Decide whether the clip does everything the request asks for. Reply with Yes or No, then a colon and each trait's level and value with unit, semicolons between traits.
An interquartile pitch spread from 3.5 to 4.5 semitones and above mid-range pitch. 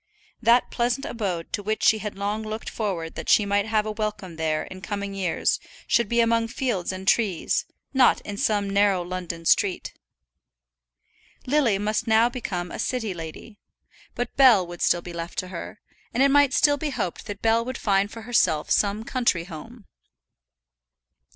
Yes: average, 3.9 semitones; high, 210 Hz